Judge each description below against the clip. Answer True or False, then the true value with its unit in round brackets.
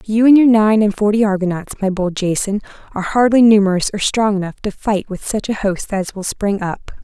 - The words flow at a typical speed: False (220 wpm)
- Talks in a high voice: True (205 Hz)